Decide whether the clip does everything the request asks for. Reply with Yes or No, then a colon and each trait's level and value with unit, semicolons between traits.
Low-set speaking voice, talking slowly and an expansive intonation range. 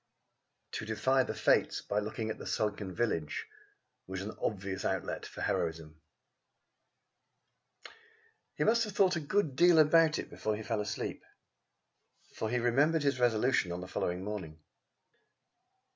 No: low, 110 Hz; average, 145 wpm; wide, 6.9 semitones